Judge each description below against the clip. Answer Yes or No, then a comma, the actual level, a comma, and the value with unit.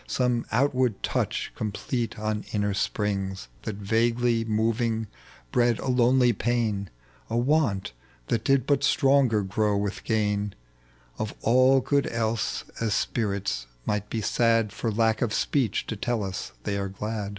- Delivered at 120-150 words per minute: Yes, average, 145 wpm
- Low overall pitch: Yes, low, 110 Hz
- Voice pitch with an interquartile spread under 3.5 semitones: Yes, average, 2.8 semitones